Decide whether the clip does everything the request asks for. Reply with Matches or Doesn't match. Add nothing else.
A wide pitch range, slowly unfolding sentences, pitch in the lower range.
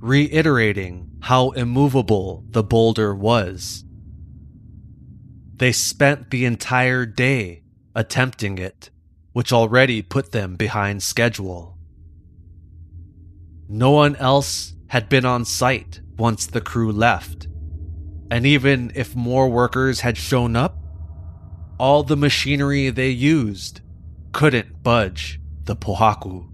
Matches